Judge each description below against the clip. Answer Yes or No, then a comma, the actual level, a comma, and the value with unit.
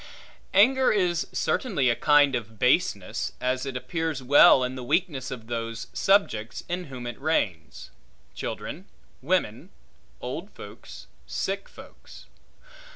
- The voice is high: No, low, 135 Hz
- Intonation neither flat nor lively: No, wide, 6.5 semitones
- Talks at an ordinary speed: No, slow, 125 wpm